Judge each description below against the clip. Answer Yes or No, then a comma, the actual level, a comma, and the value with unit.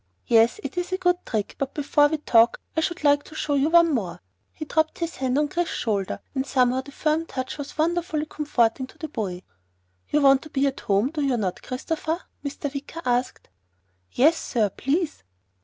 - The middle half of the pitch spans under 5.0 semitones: Yes, average, 4.0 semitones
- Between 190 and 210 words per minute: Yes, average, 200 wpm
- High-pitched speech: Yes, very high, 285 Hz